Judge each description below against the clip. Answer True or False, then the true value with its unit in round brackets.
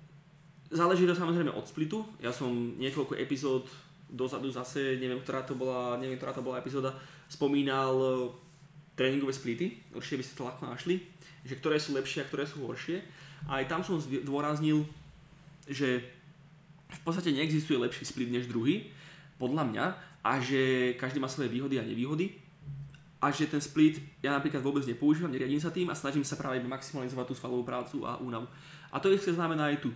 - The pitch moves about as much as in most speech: True (3.0 semitones)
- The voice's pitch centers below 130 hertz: False (140 Hz)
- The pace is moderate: False (175 wpm)